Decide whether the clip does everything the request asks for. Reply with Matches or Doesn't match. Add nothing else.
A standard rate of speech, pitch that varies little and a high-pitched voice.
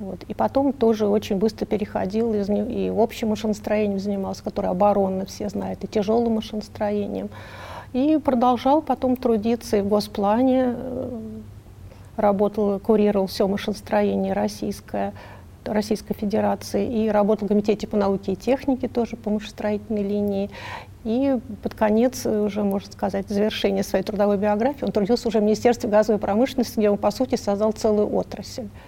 Matches